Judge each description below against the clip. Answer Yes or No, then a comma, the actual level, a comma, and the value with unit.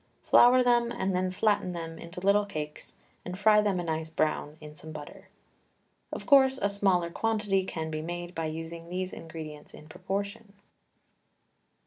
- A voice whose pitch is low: No, medium, 180 Hz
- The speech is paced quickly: No, average, 160 wpm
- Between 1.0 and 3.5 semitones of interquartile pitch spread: No, average, 4.0 semitones